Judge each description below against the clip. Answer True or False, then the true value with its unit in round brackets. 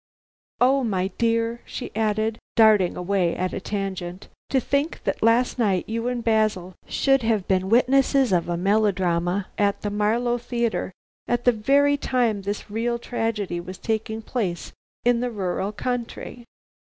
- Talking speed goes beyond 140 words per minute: True (155 wpm)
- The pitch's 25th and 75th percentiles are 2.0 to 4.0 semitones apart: True (3.7 semitones)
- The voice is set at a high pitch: True (220 Hz)